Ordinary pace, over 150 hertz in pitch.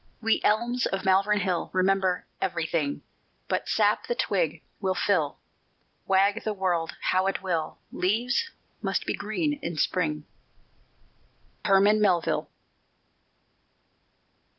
No: slow, 110 wpm; high, 190 Hz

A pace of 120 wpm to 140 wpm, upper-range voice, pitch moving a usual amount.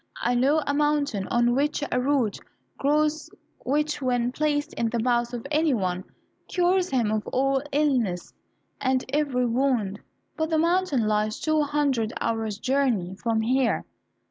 No: average, 150 wpm; very high, 260 Hz; average, 4.4 semitones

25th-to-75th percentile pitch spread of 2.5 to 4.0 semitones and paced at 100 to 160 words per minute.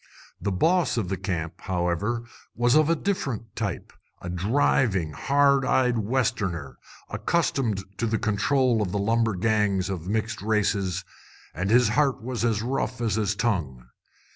No: average, 4.6 semitones; average, 145 wpm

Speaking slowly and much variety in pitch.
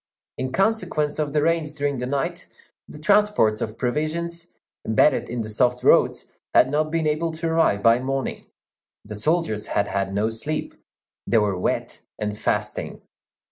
No: average, 160 wpm; wide, 6.4 semitones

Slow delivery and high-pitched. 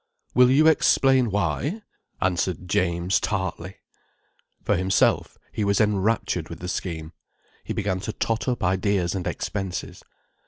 No: slow, 130 wpm; very low, 95 Hz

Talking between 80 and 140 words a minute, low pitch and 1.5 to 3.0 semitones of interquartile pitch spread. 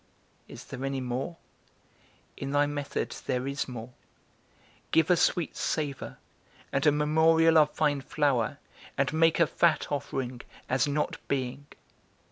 No: slow, 135 wpm; medium, 145 Hz; average, 2.7 semitones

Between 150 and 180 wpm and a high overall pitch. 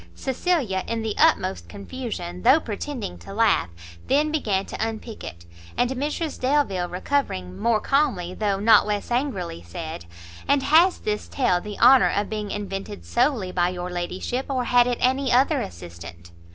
Yes: average, 160 wpm; high, 215 Hz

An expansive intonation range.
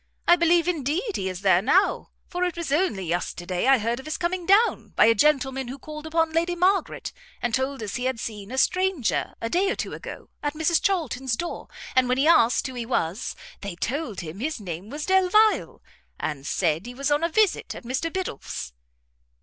Yes: wide, 7.2 semitones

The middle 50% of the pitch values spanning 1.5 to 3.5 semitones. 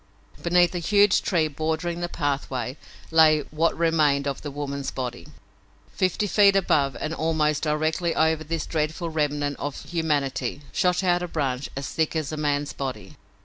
Yes: average, 2.8 semitones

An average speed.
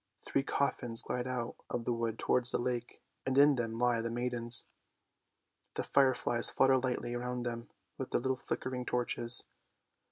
Yes: average, 165 wpm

